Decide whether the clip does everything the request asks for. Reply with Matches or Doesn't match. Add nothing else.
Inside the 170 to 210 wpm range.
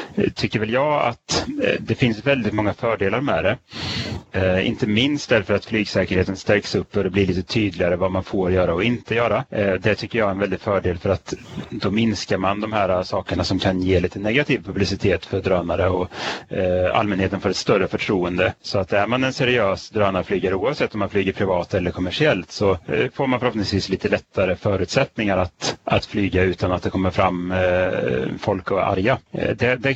Matches